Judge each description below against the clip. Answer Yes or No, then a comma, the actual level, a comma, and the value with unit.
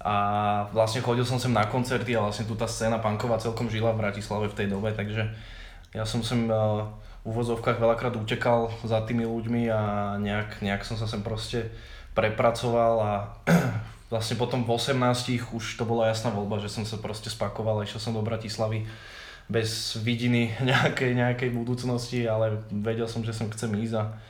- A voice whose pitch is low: Yes, low, 115 Hz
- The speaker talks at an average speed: No, fast, 180 wpm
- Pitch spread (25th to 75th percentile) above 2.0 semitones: No, narrow, 1.7 semitones